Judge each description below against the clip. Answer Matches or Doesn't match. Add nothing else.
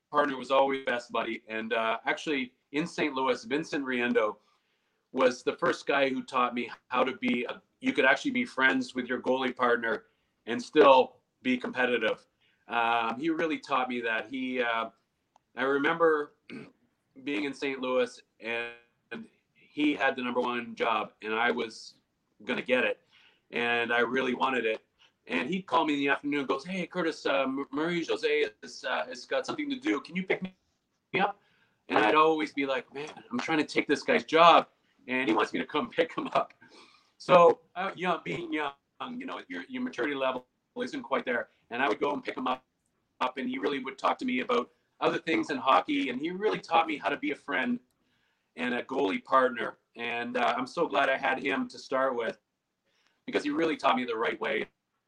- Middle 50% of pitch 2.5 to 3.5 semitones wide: Doesn't match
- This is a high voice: Doesn't match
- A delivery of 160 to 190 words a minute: Doesn't match